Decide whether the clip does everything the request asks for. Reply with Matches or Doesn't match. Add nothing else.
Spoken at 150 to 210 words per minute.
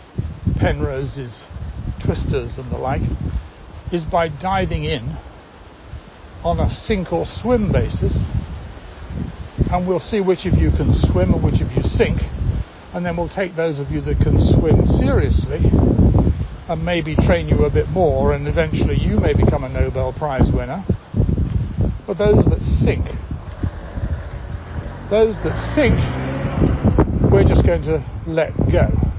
Doesn't match